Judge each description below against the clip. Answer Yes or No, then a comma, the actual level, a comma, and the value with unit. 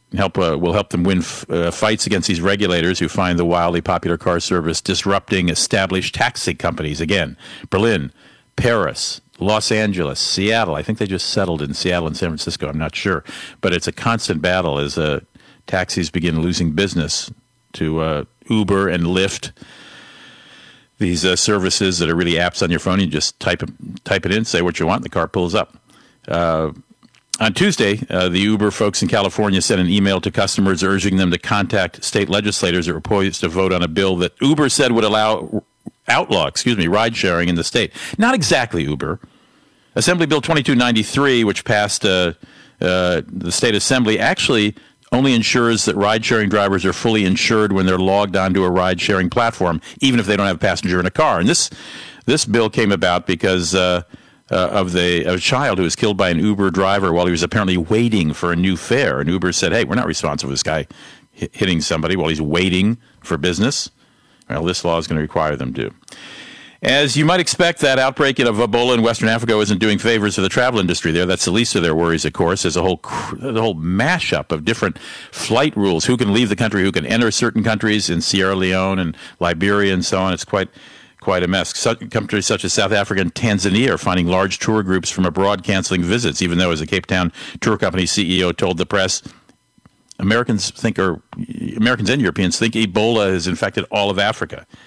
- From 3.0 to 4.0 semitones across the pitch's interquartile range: Yes, average, 3.6 semitones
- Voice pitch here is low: Yes, very low, 95 Hz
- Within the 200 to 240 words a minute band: Yes, fast, 205 wpm